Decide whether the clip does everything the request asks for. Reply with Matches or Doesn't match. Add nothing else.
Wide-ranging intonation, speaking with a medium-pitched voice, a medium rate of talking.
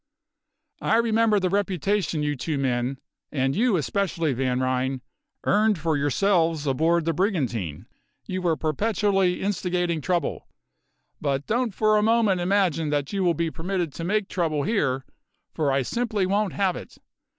Matches